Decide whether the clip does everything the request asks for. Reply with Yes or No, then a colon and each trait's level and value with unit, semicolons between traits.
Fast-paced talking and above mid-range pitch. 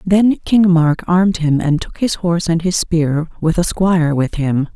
No: fast, 215 wpm; medium, 170 Hz